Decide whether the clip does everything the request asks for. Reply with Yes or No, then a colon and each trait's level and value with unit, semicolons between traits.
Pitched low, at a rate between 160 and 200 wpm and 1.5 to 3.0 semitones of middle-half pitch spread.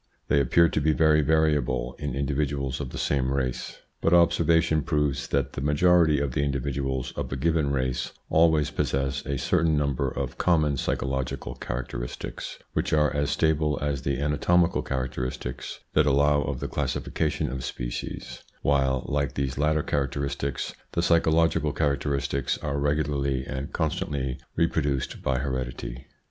No: very low, 70 Hz; average, 150 wpm; narrow, 2.4 semitones